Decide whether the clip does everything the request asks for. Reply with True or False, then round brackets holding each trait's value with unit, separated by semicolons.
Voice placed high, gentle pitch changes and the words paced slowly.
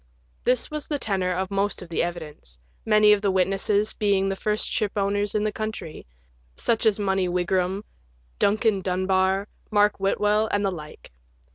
False (195 Hz; 2.2 semitones; 165 wpm)